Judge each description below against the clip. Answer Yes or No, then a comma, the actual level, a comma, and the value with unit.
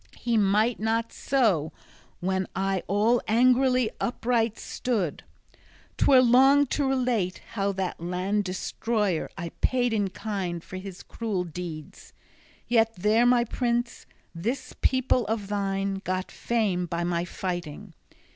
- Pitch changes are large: No, average, 4.4 semitones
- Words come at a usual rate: No, slow, 130 wpm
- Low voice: No, high, 210 Hz